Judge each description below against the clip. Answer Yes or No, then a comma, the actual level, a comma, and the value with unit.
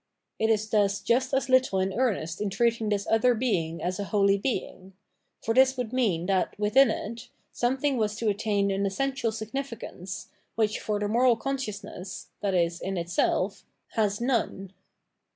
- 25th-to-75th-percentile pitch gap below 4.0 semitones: Yes, average, 3.6 semitones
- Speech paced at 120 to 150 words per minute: No, average, 160 wpm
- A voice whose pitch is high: Yes, high, 215 Hz